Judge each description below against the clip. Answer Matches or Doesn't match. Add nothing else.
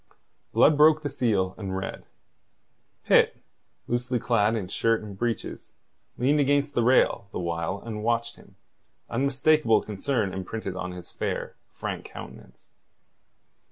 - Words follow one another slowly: Matches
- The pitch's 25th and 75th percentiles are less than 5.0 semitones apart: Doesn't match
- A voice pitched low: Matches